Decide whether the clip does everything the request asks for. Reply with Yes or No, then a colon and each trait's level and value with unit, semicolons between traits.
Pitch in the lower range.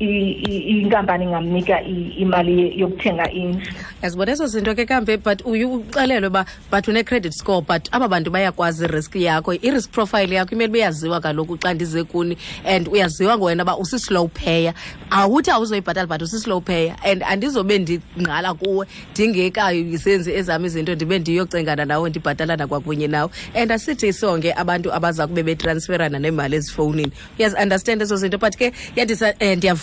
No: medium, 185 Hz